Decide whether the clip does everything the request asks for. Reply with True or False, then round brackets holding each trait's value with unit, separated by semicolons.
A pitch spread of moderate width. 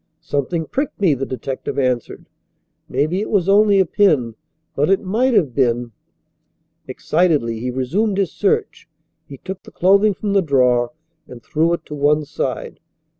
False (7.1 semitones)